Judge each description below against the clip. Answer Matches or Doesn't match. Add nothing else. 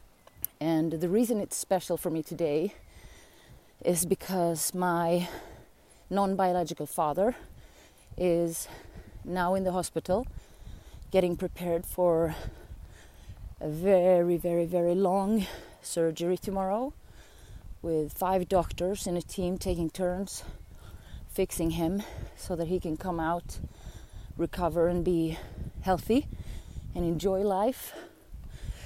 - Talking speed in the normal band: Doesn't match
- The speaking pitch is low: Doesn't match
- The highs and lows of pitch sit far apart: Doesn't match